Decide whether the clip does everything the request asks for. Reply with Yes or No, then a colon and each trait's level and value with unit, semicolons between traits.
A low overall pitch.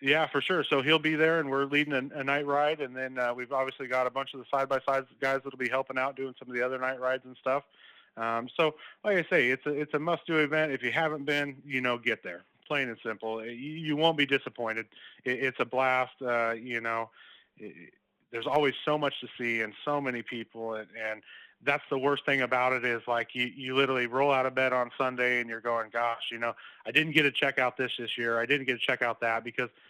Yes: low, 130 Hz